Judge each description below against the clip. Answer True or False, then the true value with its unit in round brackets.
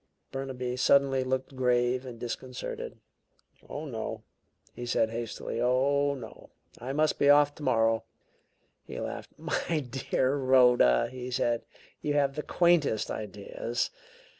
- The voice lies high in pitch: False (130 Hz)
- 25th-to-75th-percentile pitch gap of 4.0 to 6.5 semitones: False (2.7 semitones)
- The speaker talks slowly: True (125 wpm)